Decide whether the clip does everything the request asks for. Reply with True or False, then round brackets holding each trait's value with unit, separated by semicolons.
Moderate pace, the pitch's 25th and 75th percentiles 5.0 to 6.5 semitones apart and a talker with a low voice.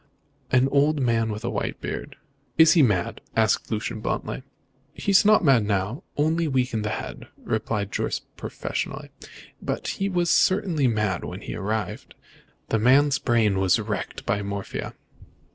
True (160 wpm; 5.6 semitones; 115 Hz)